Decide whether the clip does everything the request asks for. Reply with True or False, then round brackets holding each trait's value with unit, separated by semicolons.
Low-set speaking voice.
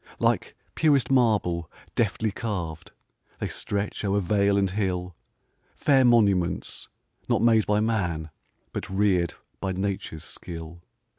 True (100 Hz)